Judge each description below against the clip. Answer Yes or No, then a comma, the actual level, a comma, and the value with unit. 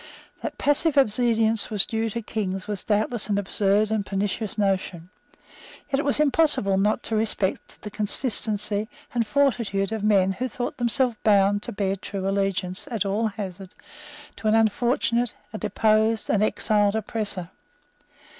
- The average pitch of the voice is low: No, high, 215 Hz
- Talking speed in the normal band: Yes, average, 150 wpm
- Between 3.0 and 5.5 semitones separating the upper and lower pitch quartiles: No, narrow, 2.4 semitones